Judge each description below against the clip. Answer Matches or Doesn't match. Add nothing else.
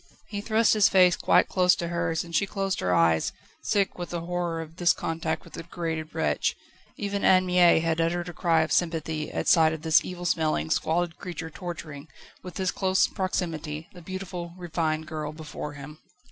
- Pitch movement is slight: Matches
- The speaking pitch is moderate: Matches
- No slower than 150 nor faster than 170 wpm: Doesn't match